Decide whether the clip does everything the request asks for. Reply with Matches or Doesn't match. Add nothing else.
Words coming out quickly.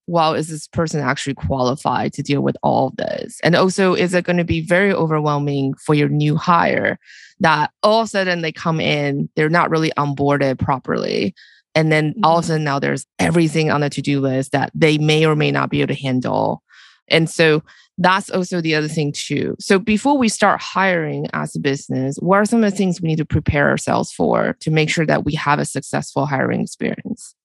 Matches